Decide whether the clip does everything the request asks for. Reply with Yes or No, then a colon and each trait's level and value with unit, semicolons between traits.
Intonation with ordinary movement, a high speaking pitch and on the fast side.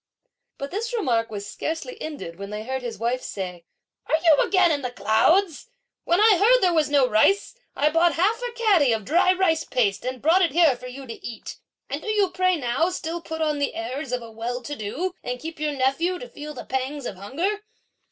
No: wide, 6.4 semitones; very high, 300 Hz; fast, 225 wpm